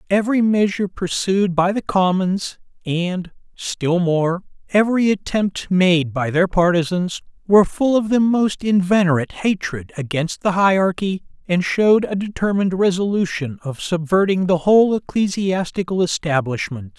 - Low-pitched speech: No, medium, 185 Hz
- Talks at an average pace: No, slow, 125 wpm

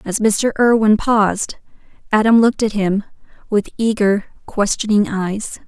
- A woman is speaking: Yes, female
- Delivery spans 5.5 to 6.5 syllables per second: No, 4.6 syllables/s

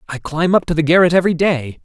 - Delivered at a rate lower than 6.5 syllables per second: No, 6.7 syllables/s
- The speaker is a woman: No, male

